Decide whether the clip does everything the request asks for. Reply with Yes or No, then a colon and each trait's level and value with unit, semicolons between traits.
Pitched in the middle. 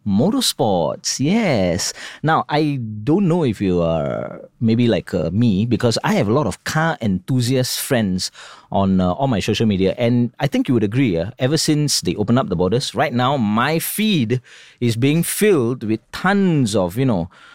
No: low, 120 Hz